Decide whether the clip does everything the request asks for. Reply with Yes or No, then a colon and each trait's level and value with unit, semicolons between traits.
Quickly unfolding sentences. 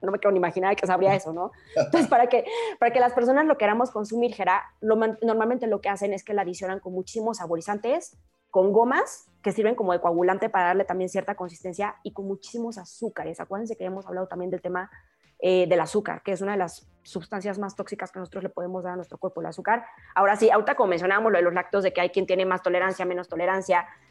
Yes: fast, 235 wpm